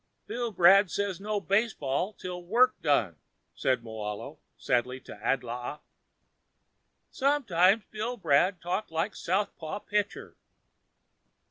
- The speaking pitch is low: No, medium, 185 Hz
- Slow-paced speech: Yes, slow, 95 wpm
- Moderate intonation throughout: No, wide, 7.0 semitones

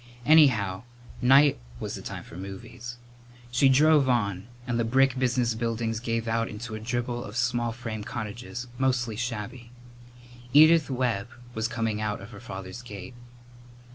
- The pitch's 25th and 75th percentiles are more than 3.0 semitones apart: No, narrow, 2.6 semitones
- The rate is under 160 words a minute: Yes, average, 150 wpm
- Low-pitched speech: Yes, low, 120 Hz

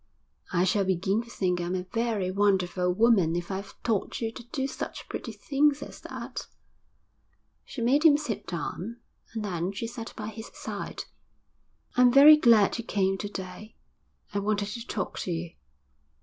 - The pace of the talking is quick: No, average, 170 wpm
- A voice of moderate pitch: No, high, 205 Hz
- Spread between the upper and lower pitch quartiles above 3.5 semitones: Yes, average, 4.0 semitones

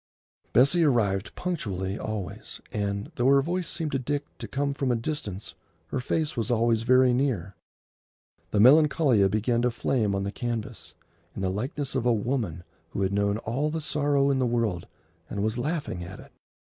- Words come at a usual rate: Yes, average, 180 wpm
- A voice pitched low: Yes, low, 120 Hz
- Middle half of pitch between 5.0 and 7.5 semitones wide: Yes, wide, 5.5 semitones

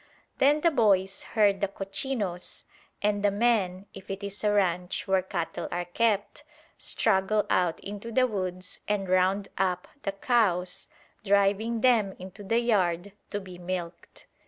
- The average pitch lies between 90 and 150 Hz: No, high, 195 Hz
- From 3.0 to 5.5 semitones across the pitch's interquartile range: No, narrow, 2.5 semitones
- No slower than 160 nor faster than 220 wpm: No, average, 150 wpm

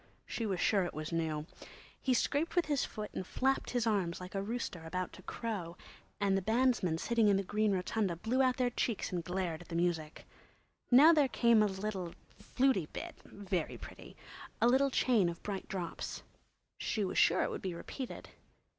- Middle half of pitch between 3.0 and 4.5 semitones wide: No, average, 5.3 semitones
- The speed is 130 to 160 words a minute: No, average, 185 wpm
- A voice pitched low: No, high, 200 Hz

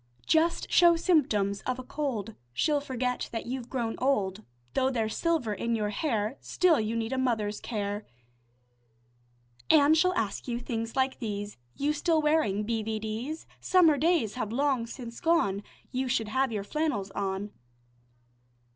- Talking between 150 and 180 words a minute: Yes, average, 155 wpm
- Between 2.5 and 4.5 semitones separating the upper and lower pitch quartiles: No, wide, 5.4 semitones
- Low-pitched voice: No, high, 240 Hz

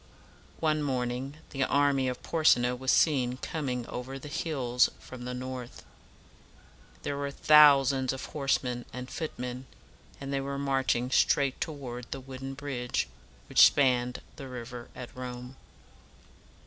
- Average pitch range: No, narrow, 2.0 semitones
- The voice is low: Yes, low, 130 Hz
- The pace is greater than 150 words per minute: No, average, 140 wpm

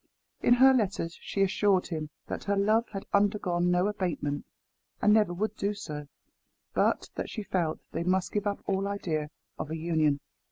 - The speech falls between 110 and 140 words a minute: No, average, 175 wpm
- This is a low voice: No, high, 190 Hz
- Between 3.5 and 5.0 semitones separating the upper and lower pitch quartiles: Yes, average, 3.8 semitones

